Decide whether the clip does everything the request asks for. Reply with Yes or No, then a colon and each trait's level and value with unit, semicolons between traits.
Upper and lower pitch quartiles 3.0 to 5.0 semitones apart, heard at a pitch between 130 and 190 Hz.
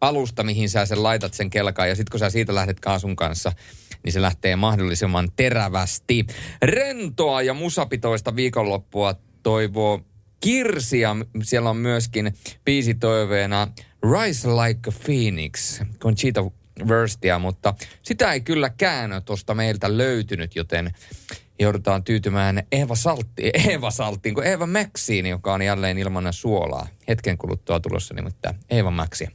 No: average, 3.3 semitones; low, 110 Hz